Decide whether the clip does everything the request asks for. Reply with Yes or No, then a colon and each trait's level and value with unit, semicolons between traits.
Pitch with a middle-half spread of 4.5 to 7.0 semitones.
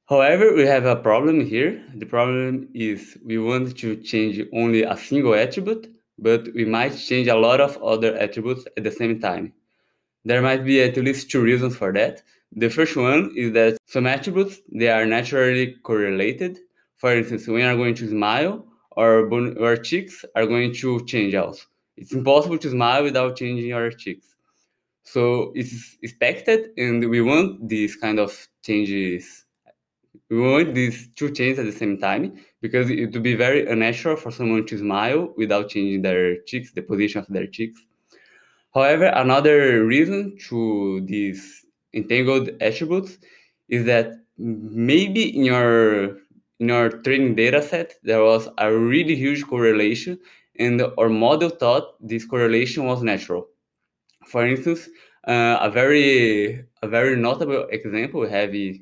No: average, 2.8 semitones